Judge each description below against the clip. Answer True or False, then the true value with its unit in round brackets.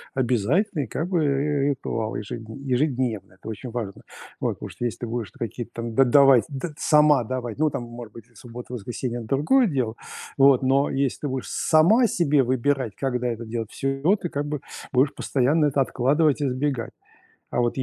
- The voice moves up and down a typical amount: True (3.5 semitones)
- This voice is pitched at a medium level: False (130 Hz)